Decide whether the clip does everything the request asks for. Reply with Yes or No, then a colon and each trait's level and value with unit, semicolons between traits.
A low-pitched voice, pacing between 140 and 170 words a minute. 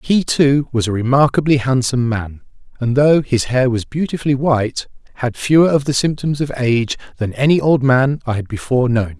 No: low, 130 Hz; average, 190 wpm